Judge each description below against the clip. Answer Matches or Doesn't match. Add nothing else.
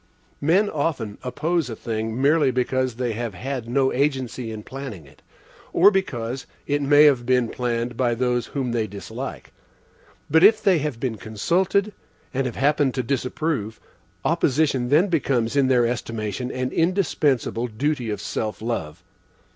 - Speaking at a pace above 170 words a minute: Doesn't match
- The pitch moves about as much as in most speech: Matches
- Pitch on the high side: Doesn't match